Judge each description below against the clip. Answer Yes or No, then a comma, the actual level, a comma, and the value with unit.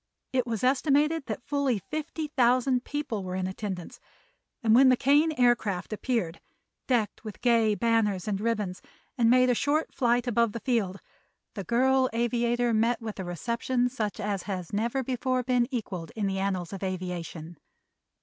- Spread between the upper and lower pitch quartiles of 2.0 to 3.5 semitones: No, average, 4.2 semitones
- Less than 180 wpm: Yes, average, 165 wpm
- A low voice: No, high, 235 Hz